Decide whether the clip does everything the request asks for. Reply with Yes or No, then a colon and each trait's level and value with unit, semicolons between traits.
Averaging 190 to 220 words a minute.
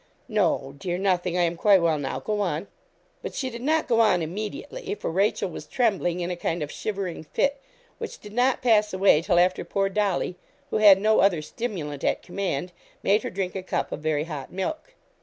Yes: fast, 205 wpm